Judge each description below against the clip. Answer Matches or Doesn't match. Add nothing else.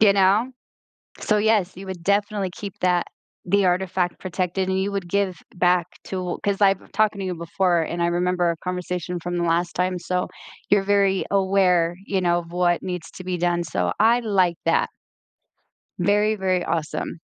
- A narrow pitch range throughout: Matches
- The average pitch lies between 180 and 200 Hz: Matches